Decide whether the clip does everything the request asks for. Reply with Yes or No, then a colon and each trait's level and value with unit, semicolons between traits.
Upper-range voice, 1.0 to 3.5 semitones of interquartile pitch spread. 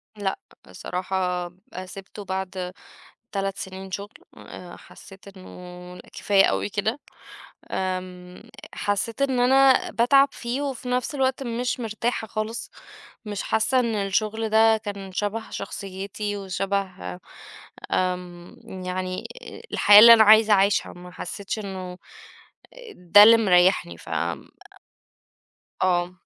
Yes: high, 200 Hz; average, 3.2 semitones